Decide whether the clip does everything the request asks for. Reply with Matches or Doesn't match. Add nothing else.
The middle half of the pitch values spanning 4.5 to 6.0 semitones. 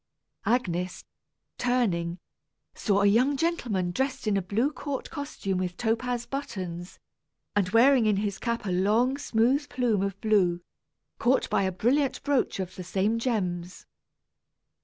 Matches